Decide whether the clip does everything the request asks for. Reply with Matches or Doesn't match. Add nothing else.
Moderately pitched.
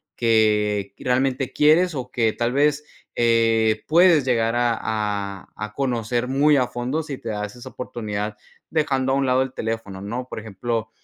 Doesn't match